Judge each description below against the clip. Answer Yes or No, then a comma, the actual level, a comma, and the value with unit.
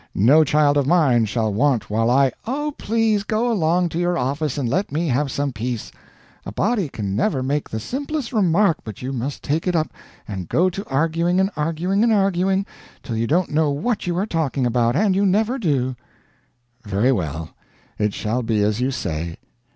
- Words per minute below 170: No, average, 195 wpm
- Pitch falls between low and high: Yes, medium, 150 Hz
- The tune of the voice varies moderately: No, wide, 7.6 semitones